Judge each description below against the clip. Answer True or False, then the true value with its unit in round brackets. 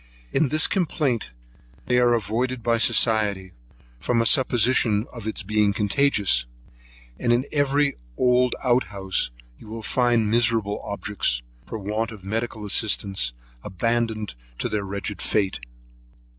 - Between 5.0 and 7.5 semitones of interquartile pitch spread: False (3.1 semitones)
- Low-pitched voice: True (110 Hz)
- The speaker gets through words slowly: True (130 wpm)